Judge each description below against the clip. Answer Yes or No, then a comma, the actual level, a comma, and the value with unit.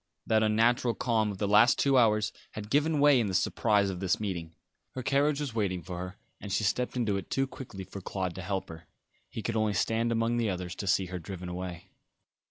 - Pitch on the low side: Yes, low, 105 Hz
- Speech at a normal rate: No, fast, 225 wpm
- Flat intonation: No, average, 4.1 semitones